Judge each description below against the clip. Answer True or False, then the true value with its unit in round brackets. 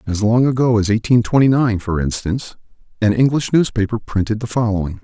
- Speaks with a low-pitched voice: True (110 Hz)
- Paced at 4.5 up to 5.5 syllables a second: False (5.8 syllables/s)